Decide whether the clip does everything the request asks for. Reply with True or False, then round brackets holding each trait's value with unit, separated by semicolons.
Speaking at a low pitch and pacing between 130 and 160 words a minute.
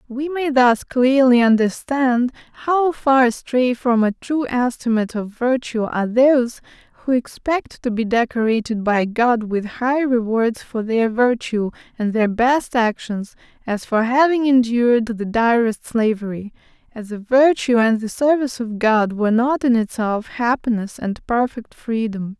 False (240 Hz; 150 wpm)